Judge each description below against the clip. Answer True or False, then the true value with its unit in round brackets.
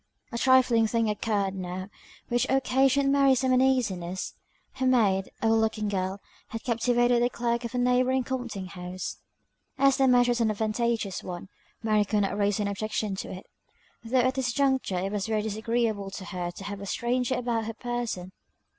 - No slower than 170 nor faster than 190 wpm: True (180 wpm)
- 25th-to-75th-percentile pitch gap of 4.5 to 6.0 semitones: False (3.7 semitones)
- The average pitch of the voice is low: False (225 Hz)